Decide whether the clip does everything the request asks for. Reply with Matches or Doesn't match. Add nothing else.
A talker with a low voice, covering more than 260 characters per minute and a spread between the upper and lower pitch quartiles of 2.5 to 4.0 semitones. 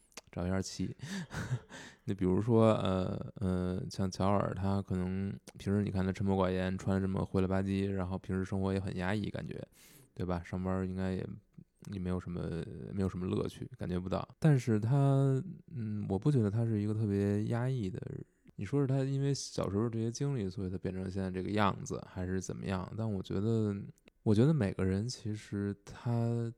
Matches